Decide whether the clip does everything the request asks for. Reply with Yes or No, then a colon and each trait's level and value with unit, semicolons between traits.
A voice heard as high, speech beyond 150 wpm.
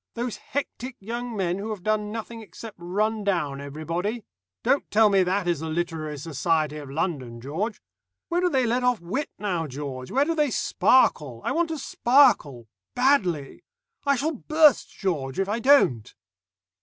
Yes: high, 200 Hz; average, 170 wpm